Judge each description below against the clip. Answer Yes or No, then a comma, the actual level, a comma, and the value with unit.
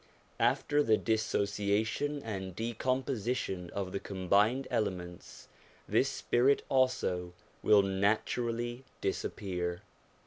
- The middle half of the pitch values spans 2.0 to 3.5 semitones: No, average, 4.2 semitones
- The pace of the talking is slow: Yes, slow, 95 wpm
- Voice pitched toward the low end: Yes, low, 105 Hz